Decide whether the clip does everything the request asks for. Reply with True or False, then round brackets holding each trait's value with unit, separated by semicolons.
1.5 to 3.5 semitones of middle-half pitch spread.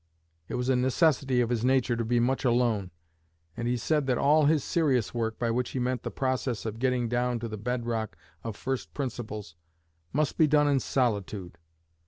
True (2.4 semitones)